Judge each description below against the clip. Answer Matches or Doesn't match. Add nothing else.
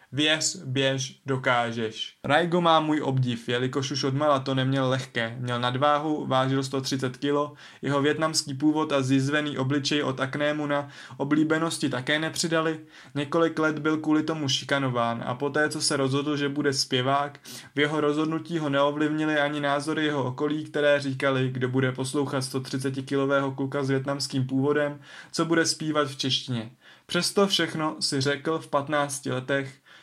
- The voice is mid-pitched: Matches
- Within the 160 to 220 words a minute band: Doesn't match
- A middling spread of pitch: Doesn't match